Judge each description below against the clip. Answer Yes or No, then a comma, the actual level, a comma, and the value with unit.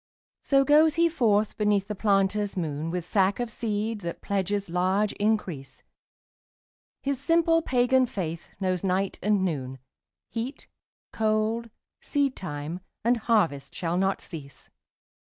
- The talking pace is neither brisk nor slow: No, slow, 125 wpm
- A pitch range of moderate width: Yes, average, 4.5 semitones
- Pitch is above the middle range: Yes, high, 205 Hz